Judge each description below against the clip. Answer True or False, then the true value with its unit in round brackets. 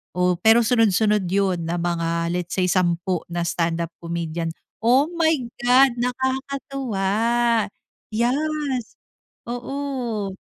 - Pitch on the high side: True (210 Hz)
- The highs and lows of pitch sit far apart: True (6.8 semitones)